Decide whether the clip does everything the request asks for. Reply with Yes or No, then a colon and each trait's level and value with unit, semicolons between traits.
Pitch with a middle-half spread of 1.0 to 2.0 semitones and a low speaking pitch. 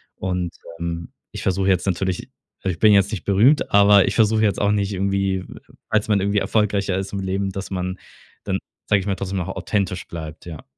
Yes: narrow, 1.7 semitones; very low, 95 Hz